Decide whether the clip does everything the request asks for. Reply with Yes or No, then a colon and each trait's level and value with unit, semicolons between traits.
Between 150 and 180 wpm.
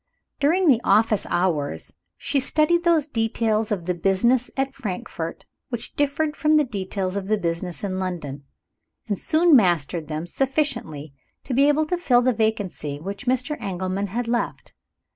Yes: average, 160 wpm